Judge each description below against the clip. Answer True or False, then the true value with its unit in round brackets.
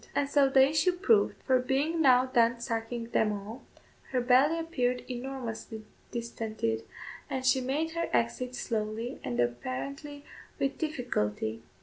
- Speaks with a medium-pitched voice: False (250 Hz)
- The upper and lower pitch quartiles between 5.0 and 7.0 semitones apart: False (3.5 semitones)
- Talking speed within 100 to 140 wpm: True (135 wpm)